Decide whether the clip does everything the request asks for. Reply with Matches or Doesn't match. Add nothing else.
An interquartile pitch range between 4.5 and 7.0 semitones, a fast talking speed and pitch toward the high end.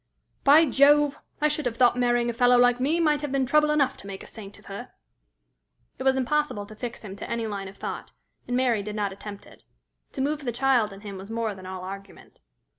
Matches